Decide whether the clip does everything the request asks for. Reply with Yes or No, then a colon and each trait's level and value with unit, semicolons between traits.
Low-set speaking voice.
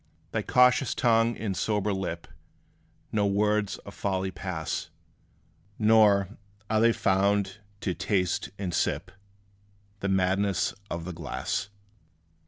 Yes: low, 100 Hz